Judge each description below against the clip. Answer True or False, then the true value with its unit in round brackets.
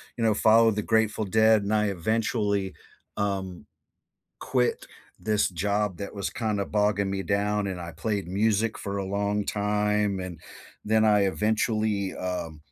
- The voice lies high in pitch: False (105 Hz)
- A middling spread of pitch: False (1.8 semitones)